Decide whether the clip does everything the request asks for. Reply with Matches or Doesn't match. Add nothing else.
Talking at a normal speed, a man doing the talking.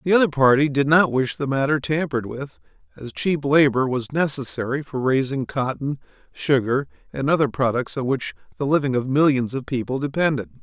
Matches